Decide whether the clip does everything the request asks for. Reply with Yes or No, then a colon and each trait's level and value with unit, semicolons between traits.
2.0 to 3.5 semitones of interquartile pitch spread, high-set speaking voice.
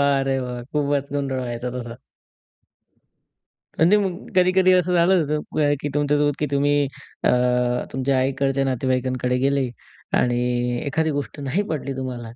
No: narrow, 2.5 semitones; medium, 140 Hz